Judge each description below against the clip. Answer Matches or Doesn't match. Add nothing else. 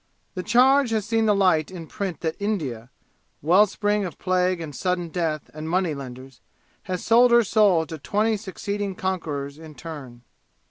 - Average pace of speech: Matches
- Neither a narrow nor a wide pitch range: Matches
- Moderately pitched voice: Matches